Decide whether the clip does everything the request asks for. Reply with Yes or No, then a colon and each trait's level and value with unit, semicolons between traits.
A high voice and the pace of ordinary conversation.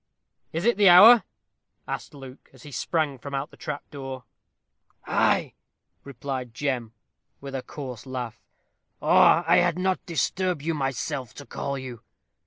No: medium, 140 Hz; average, 145 wpm